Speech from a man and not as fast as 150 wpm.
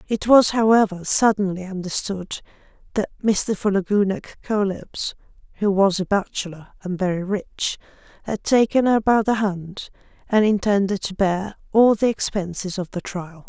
No: female; average, 140 wpm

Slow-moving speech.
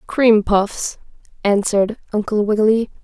Yes: slow, 100 wpm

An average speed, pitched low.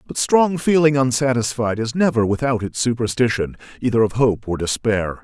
Yes: average, 160 wpm; low, 120 Hz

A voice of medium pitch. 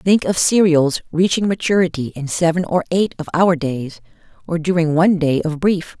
Yes: medium, 170 Hz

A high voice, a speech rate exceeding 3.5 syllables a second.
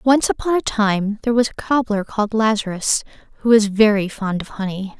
Yes: high, 215 Hz; 5.4 syllables/s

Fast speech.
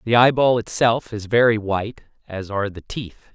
No: average, 180 wpm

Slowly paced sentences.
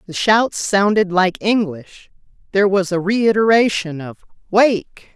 Yes: slow, 130 wpm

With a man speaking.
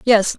No: female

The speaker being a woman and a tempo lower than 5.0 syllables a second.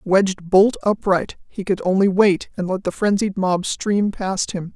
Yes: female; 4.3 syllables/s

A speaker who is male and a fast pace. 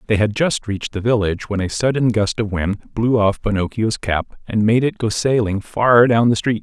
Yes: male; fast, 225 wpm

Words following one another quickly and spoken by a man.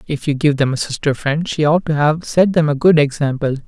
Yes: fast, 260 wpm; male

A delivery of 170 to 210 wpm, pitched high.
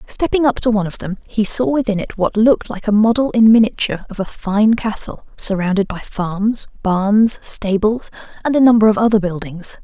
Yes: average, 195 wpm; high, 210 Hz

